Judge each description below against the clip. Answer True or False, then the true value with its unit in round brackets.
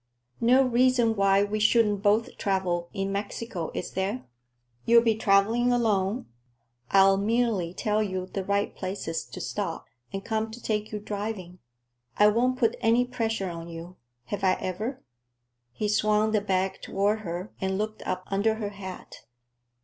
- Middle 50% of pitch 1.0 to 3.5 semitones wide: True (2.7 semitones)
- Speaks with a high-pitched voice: True (205 Hz)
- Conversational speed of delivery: True (155 wpm)